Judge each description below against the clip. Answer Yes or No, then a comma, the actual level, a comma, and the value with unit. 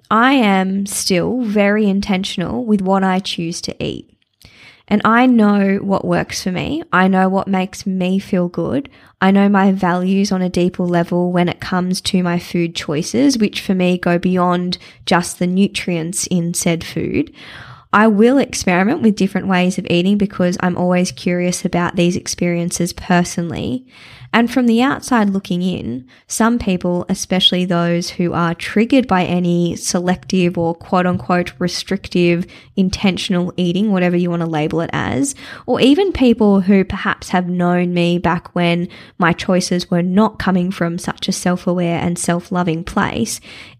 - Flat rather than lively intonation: Yes, narrow, 2.1 semitones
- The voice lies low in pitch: No, medium, 180 Hz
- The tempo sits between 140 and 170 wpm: Yes, average, 165 wpm